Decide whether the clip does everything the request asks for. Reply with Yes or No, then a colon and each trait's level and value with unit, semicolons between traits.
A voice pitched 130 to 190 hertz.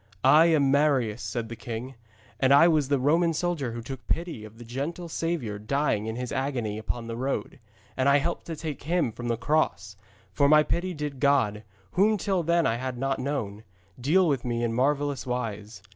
Yes: low, 135 Hz